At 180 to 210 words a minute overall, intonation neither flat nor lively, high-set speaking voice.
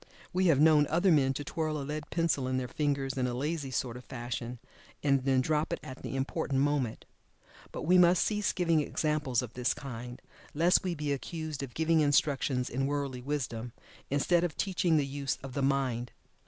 No: average, 195 wpm; average, 3.5 semitones; medium, 140 Hz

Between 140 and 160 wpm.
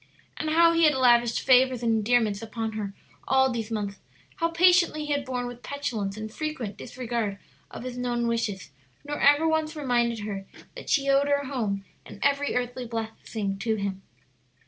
No: average, 175 wpm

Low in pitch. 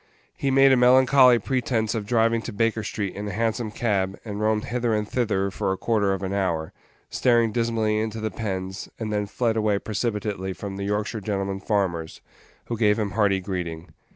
Yes: low, 105 Hz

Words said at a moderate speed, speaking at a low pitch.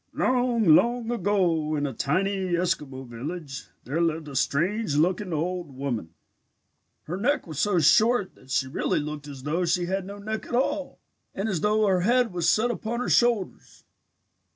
No: average, 175 wpm; medium, 180 Hz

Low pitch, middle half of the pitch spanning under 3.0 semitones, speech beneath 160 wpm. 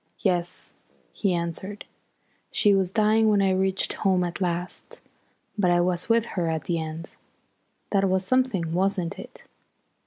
No: medium, 185 Hz; narrow, 2.5 semitones; average, 150 wpm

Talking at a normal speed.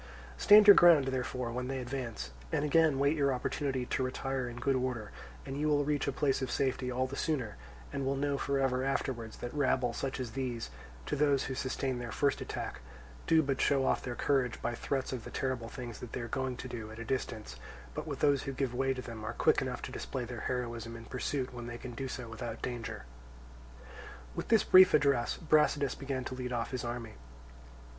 No: fast, 220 wpm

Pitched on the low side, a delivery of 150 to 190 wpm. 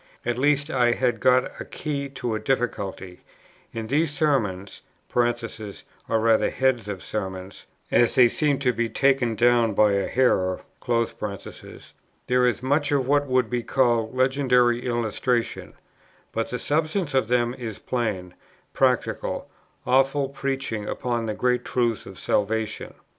No: low, 120 Hz; average, 140 wpm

